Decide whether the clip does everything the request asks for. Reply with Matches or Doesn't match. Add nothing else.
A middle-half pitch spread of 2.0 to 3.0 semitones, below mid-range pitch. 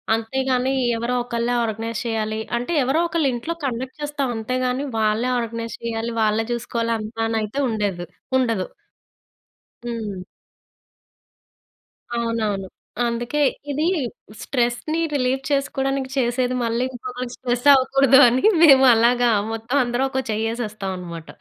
Doesn't match